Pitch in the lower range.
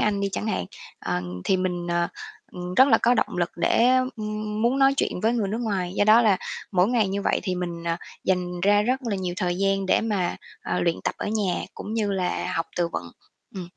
No: high, 195 Hz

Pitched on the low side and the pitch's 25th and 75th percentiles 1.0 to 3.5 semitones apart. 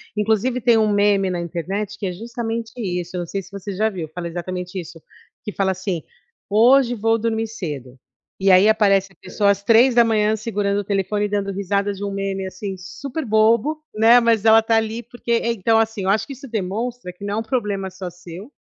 No: high, 205 Hz; average, 2.9 semitones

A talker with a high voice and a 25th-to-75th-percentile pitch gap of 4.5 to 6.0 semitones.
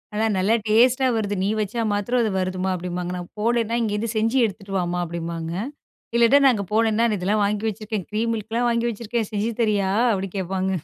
No: high, 210 Hz; average, 3.3 semitones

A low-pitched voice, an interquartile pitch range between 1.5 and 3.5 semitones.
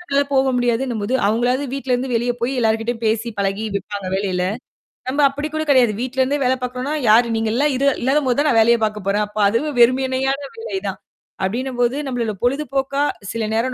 No: high, 245 Hz; average, 3.1 semitones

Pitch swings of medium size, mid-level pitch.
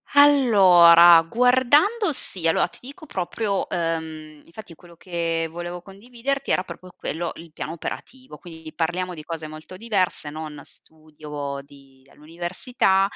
Yes: average, 5.0 semitones; medium, 175 Hz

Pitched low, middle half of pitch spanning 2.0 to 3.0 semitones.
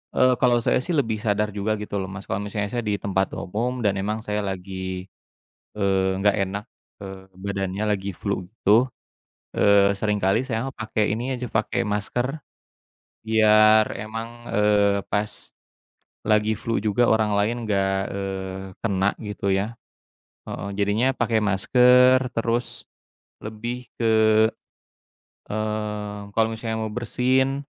Yes: low, 105 Hz; narrow, 2.4 semitones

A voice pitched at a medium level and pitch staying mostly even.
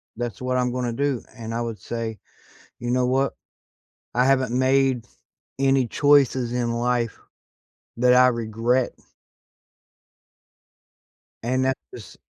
No: low, 125 Hz; narrow, 1.7 semitones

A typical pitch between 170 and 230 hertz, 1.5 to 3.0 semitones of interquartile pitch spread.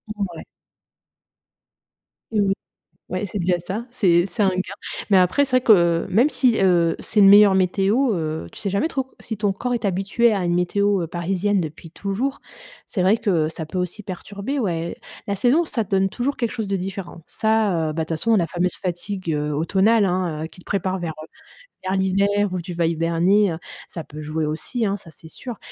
No: high, 190 Hz; average, 3.4 semitones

